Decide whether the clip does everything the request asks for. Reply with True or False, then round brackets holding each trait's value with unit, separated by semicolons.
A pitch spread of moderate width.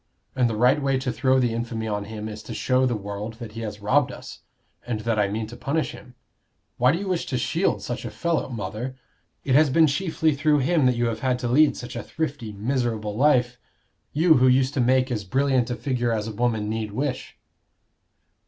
True (3.6 semitones)